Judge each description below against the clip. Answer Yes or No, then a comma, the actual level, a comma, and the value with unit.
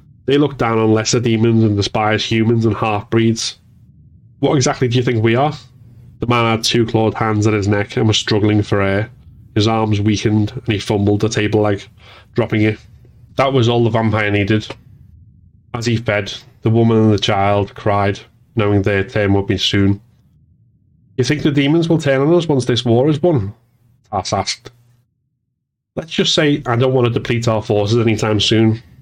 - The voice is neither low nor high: No, low, 115 Hz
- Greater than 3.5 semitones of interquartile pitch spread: No, average, 2.7 semitones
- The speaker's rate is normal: Yes, average, 190 wpm